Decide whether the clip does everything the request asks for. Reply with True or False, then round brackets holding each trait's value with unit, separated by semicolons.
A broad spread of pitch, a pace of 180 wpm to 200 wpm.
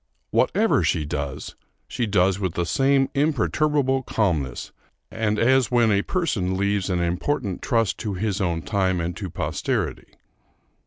False (5.9 semitones; 145 wpm)